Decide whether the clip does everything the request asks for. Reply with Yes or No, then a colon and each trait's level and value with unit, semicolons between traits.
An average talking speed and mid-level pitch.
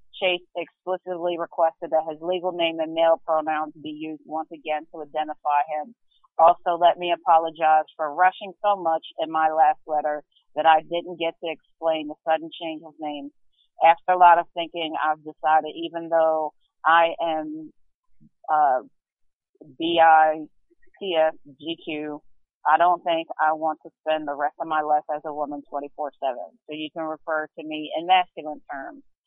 Yes: average, 170 wpm; medium, 160 Hz